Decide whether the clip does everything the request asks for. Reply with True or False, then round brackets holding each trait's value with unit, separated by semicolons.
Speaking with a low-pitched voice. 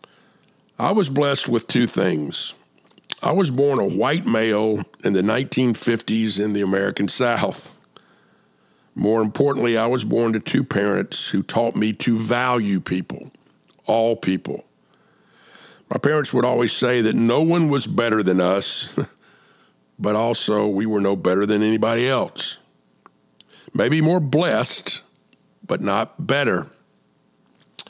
True (115 Hz)